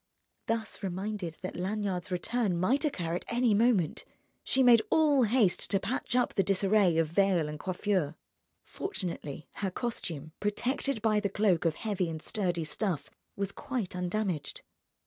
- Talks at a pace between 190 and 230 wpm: No, average, 150 wpm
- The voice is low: No, high, 195 Hz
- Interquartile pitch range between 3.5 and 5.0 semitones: Yes, average, 4.0 semitones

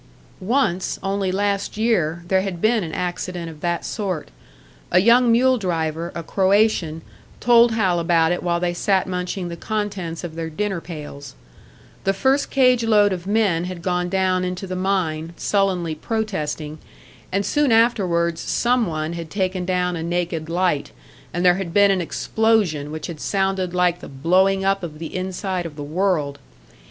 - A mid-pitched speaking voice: Yes, medium, 180 Hz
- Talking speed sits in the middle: Yes, average, 170 wpm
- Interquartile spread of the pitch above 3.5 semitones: No, average, 3.1 semitones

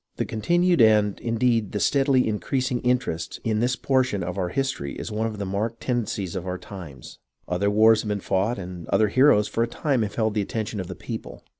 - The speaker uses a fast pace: Yes, fast, 210 wpm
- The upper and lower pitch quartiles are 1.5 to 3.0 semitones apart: No, average, 3.8 semitones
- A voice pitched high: No, low, 110 Hz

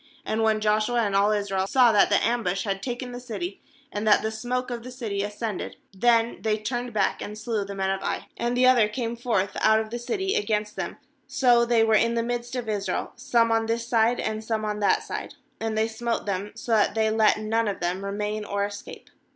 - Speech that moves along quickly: Yes, fast, 235 wpm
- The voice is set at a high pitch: Yes, high, 220 Hz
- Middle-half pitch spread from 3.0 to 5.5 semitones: No, narrow, 2.4 semitones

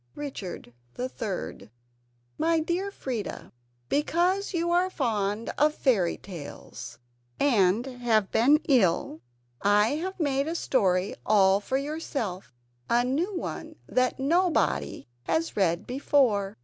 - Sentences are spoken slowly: Yes, slow, 115 wpm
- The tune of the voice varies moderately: No, wide, 7.6 semitones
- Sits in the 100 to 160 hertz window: No, very high, 255 Hz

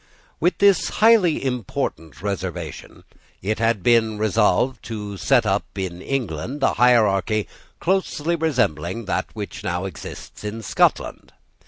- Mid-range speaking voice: No, low, 110 Hz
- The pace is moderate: No, slow, 125 wpm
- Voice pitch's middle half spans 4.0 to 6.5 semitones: Yes, wide, 5.6 semitones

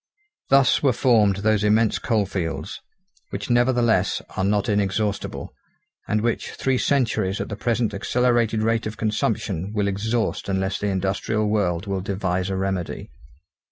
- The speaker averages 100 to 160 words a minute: Yes, average, 140 wpm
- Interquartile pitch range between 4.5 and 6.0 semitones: No, average, 2.8 semitones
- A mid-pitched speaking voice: No, low, 105 Hz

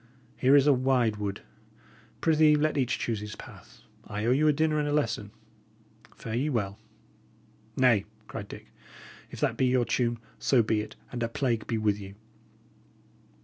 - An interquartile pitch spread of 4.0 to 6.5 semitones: Yes, average, 4.7 semitones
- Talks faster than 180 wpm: No, average, 175 wpm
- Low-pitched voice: Yes, low, 120 Hz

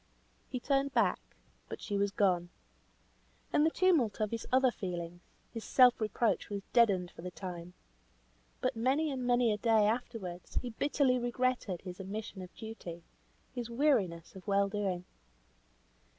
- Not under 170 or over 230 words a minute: No, average, 150 wpm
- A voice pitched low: No, high, 220 Hz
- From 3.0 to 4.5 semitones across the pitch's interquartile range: No, average, 5.1 semitones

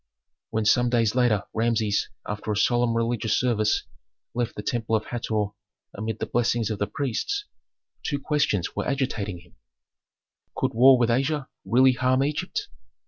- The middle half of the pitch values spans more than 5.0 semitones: No, average, 3.0 semitones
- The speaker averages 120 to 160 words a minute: Yes, average, 150 wpm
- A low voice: Yes, low, 115 Hz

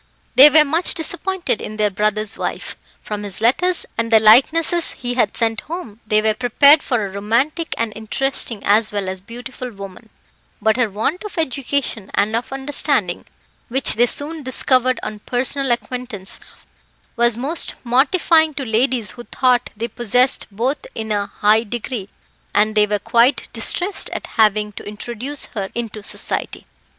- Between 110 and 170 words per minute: Yes, average, 160 wpm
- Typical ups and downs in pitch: Yes, average, 4.2 semitones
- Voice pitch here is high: Yes, high, 235 Hz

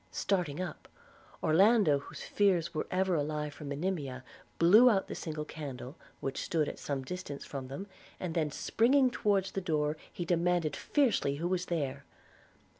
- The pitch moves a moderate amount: Yes, average, 4.4 semitones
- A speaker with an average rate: Yes, average, 160 wpm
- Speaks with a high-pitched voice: No, medium, 165 Hz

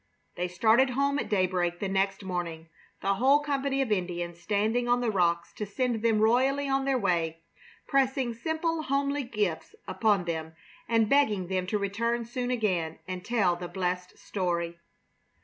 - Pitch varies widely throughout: Yes, wide, 5.9 semitones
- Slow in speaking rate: No, average, 165 wpm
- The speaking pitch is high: Yes, high, 210 Hz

